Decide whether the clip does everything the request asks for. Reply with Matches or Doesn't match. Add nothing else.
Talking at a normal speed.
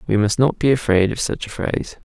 Doesn't match